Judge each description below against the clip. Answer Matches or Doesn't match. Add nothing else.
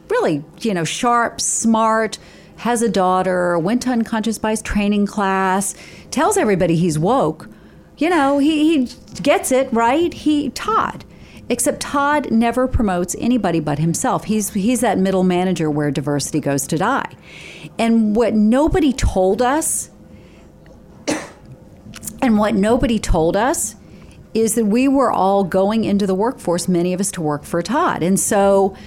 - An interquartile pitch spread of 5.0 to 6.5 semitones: Matches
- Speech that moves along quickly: Doesn't match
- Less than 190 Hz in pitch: Doesn't match